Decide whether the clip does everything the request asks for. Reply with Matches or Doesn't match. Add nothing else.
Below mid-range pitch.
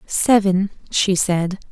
Doesn't match